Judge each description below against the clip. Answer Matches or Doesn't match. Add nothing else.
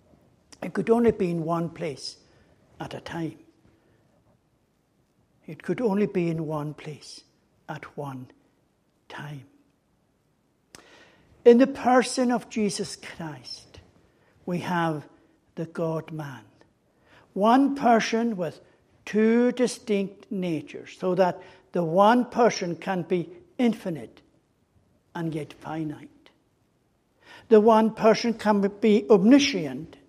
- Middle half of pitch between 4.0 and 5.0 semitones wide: Doesn't match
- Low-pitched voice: Doesn't match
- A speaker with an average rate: Doesn't match